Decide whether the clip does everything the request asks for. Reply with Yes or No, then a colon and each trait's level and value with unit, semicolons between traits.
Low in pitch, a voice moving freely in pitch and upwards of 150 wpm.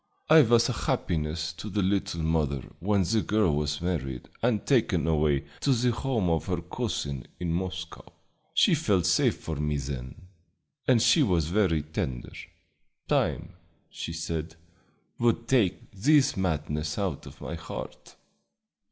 No: very low, 85 Hz; wide, 5.7 semitones; average, 145 wpm